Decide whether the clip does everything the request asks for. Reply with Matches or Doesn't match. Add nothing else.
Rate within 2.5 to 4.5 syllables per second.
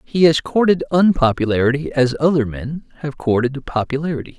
Doesn't match